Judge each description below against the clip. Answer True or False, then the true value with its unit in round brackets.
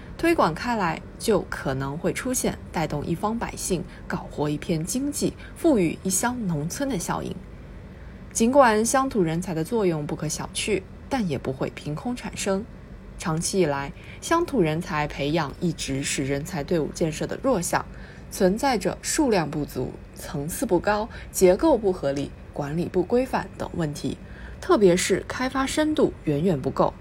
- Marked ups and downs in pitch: True (7.1 semitones)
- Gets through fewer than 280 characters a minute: True (240 characters per minute)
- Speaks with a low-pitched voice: False (180 Hz)